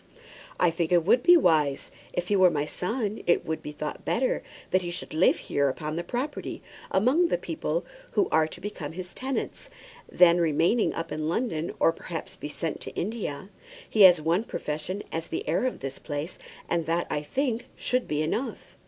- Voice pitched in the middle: Yes, medium, 175 Hz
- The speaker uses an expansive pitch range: Yes, wide, 5.9 semitones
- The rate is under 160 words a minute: No, average, 195 wpm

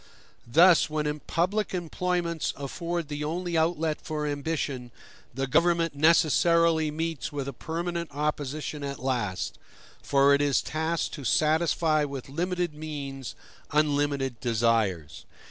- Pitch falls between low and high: Yes, medium, 150 Hz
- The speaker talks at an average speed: No, slow, 120 wpm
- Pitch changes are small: No, average, 3.1 semitones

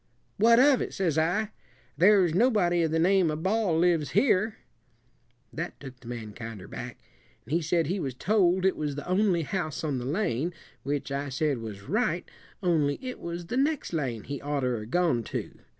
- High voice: No, medium, 165 Hz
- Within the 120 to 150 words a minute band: No, average, 190 wpm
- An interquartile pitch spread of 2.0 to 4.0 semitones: No, average, 5.3 semitones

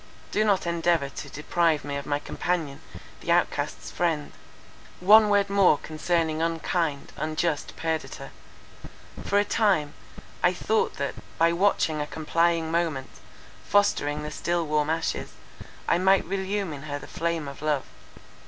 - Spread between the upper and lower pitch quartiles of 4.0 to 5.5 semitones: No, average, 3.1 semitones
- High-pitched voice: No, medium, 165 Hz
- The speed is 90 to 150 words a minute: Yes, average, 145 wpm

